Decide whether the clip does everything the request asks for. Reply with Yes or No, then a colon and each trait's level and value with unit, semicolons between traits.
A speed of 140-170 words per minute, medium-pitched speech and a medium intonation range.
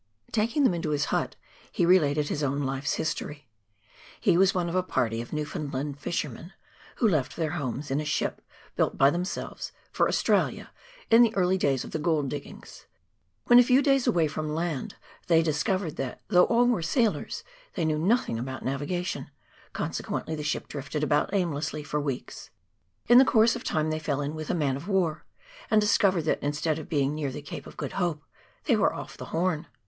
No: average, 195 wpm; medium, 155 Hz; average, 4.1 semitones